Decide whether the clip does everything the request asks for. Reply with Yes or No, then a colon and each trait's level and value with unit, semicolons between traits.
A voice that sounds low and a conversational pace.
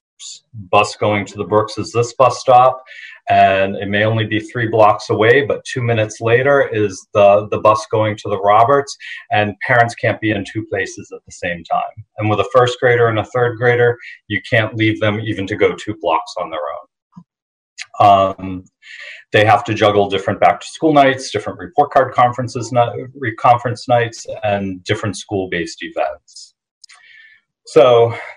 Yes: low, 110 Hz; average, 175 wpm